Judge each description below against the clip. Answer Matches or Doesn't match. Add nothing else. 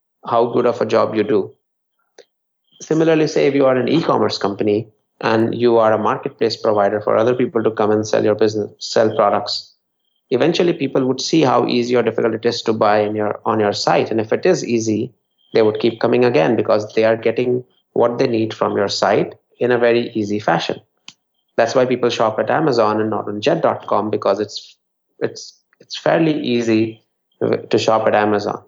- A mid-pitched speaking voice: Doesn't match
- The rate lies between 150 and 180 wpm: Doesn't match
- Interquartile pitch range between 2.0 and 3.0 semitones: Matches